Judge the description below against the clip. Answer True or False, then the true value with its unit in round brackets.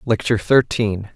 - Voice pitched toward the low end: True (110 Hz)